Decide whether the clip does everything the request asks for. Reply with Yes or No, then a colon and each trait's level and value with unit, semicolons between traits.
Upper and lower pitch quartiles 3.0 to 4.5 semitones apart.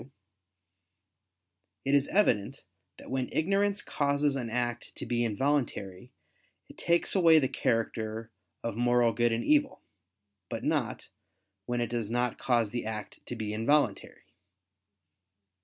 Yes: average, 3.9 semitones